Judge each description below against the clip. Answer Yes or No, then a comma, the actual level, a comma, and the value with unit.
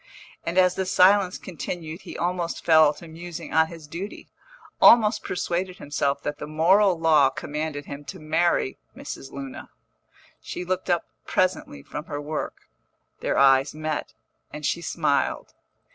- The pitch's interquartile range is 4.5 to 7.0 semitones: No, average, 3.3 semitones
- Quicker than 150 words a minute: No, average, 145 wpm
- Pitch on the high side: No, medium, 160 Hz